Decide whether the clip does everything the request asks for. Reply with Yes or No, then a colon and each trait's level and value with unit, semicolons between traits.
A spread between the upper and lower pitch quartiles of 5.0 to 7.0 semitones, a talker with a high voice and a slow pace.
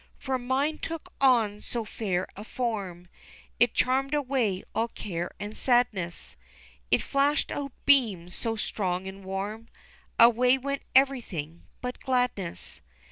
Yes: average, 5.3 semitones; high, 230 Hz; slow, 130 wpm